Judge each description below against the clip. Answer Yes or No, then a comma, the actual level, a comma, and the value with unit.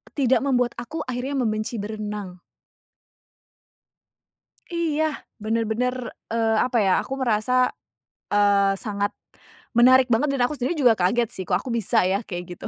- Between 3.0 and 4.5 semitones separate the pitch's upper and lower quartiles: Yes, average, 3.7 semitones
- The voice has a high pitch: Yes, high, 230 Hz